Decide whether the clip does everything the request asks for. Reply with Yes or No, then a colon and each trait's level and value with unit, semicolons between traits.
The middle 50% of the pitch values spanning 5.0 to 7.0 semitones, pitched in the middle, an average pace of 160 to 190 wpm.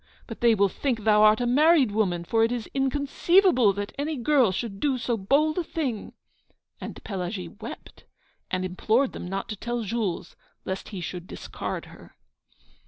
No: wide, 5.5 semitones; high, 225 Hz; average, 175 wpm